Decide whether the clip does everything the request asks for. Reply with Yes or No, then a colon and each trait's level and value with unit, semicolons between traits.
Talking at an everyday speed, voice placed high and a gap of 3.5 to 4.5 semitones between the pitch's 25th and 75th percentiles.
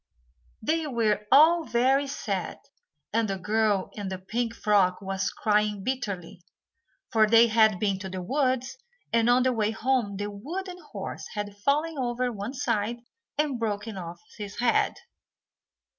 Yes: average, 155 wpm; high, 220 Hz; average, 3.9 semitones